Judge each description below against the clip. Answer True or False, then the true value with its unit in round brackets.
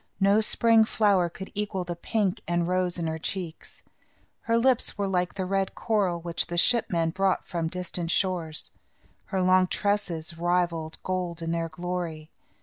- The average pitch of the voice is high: False (180 Hz)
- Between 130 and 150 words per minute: False (165 wpm)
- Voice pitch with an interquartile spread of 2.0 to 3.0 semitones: True (2.5 semitones)